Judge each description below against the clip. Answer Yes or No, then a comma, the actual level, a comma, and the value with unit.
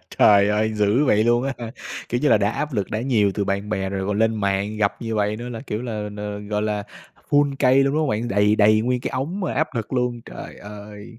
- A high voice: No, low, 110 Hz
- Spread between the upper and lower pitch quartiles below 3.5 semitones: Yes, average, 3.1 semitones